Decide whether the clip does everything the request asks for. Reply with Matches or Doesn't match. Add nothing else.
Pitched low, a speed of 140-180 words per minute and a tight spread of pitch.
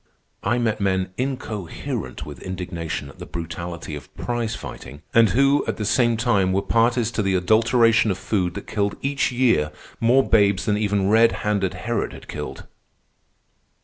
Doesn't match